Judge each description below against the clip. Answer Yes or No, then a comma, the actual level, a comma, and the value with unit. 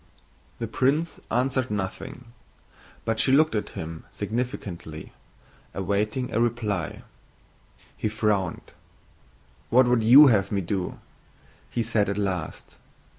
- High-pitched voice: No, low, 110 Hz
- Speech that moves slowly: Yes, slow, 115 wpm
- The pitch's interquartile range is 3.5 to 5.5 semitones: Yes, average, 4.2 semitones